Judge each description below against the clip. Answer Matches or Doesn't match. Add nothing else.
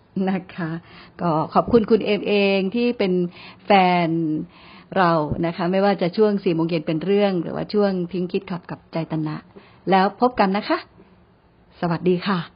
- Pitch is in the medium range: Matches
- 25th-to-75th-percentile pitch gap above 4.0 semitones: Doesn't match